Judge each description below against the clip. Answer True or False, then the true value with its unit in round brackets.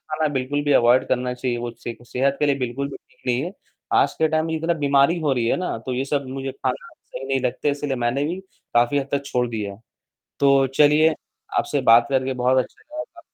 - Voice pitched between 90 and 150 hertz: True (135 Hz)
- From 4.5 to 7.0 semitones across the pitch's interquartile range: False (2.9 semitones)